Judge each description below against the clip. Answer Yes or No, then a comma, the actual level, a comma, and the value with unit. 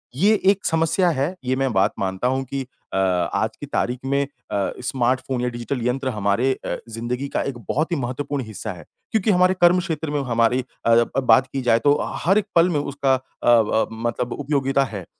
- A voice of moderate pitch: No, low, 130 Hz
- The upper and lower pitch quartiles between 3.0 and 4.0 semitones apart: Yes, average, 3.5 semitones